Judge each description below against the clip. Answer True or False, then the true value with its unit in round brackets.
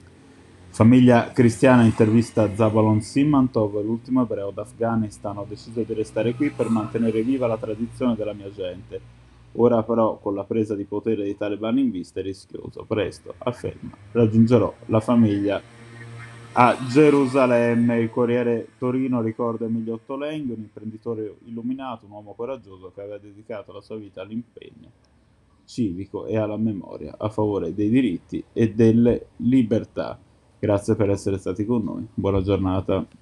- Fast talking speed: False (145 wpm)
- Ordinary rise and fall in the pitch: False (2.3 semitones)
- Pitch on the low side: True (115 Hz)